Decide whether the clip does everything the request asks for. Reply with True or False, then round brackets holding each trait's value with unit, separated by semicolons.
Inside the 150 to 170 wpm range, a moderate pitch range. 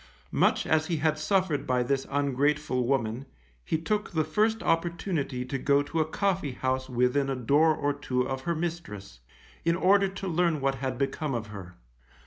False (180 wpm; 4.3 semitones)